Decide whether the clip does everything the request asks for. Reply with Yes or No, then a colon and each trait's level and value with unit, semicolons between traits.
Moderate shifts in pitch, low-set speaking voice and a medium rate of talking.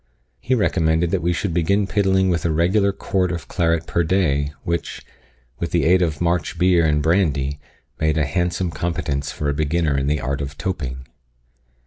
Yes: average, 3.6 semitones; very low, 85 Hz; average, 180 wpm